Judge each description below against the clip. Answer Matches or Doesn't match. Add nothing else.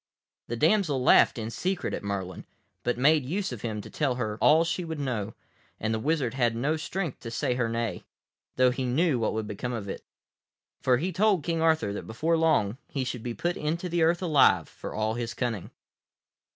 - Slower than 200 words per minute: Doesn't match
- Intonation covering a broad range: Matches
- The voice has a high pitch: Doesn't match